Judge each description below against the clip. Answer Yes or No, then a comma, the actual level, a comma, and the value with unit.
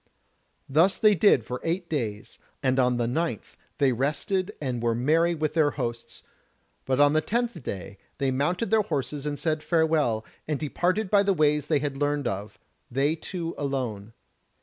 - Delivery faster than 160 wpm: Yes, average, 170 wpm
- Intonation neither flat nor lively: Yes, average, 4.6 semitones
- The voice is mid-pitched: Yes, medium, 145 Hz